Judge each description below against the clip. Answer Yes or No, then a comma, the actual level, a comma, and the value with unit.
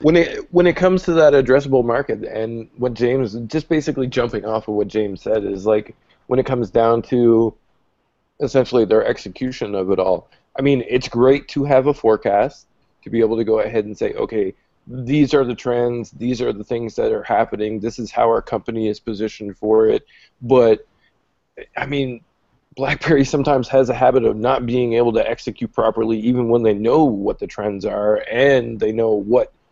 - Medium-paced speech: Yes, average, 195 wpm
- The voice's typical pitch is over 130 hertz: No, low, 120 Hz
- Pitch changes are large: No, average, 3.3 semitones